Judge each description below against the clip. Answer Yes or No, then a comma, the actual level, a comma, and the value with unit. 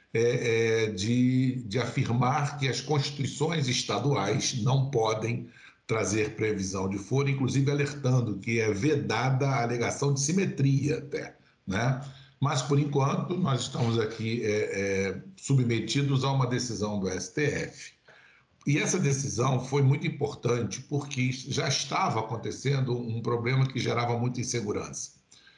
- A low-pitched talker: Yes, low, 130 Hz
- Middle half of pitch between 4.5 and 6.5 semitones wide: No, average, 3.7 semitones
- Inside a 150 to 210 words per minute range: No, average, 125 wpm